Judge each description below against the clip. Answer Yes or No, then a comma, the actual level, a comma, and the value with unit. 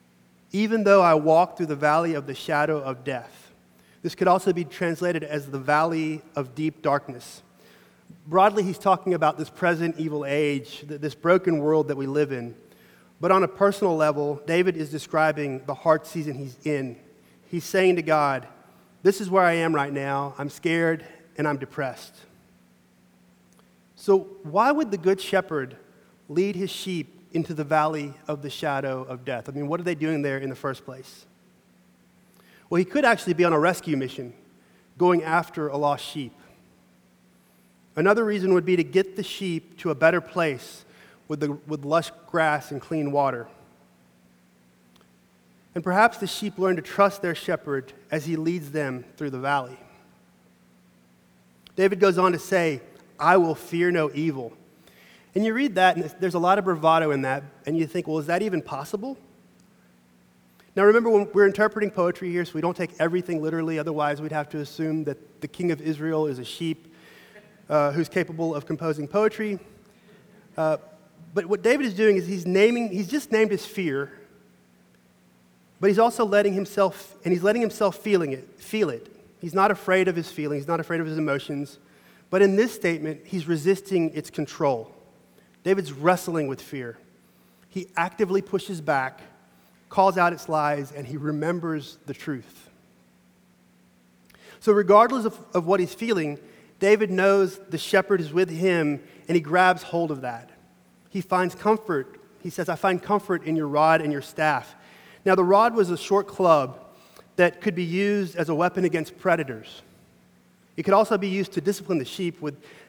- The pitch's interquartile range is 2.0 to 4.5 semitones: No, average, 4.9 semitones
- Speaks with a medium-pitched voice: Yes, medium, 160 Hz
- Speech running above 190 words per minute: No, average, 175 wpm